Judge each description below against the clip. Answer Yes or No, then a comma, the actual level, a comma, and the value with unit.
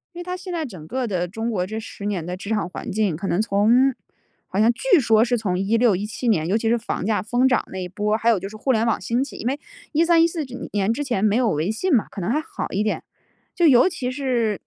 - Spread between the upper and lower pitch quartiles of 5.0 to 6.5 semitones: No, average, 4.2 semitones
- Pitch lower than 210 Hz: No, high, 225 Hz